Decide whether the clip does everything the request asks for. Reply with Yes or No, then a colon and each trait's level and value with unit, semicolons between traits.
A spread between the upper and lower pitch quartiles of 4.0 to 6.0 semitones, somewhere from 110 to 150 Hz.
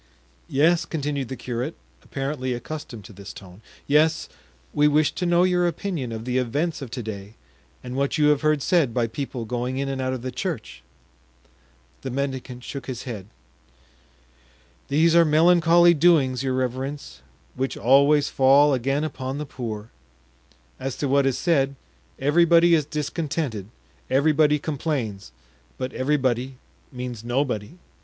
No: average, 3.4 semitones; low, 135 Hz